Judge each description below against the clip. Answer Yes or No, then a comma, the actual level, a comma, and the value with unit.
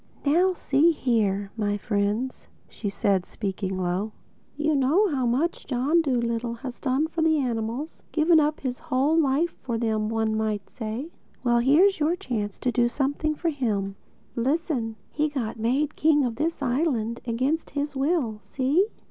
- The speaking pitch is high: Yes, very high, 255 Hz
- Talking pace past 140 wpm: Yes, average, 160 wpm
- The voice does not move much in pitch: No, average, 5.3 semitones